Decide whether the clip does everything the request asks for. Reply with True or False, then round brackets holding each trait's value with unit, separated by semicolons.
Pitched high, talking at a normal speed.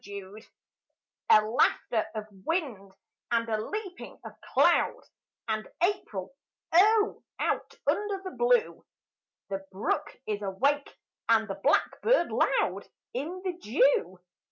False (240 Hz; 115 wpm)